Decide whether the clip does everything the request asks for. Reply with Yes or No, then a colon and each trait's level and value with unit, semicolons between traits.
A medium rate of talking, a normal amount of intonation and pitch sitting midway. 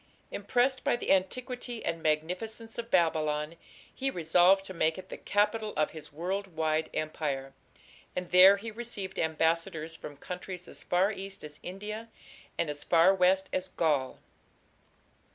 Yes: average, 150 wpm; average, 4.2 semitones; medium, 180 Hz